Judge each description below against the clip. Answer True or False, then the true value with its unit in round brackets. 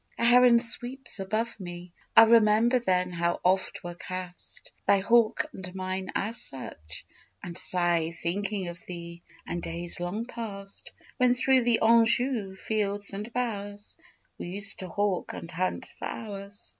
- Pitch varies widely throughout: False (4.3 semitones)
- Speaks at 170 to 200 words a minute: False (150 wpm)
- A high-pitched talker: True (200 Hz)